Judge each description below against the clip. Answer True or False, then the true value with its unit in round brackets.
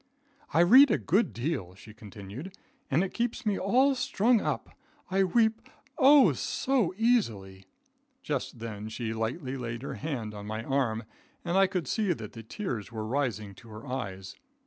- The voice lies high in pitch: False (135 Hz)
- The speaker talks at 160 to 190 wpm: True (170 wpm)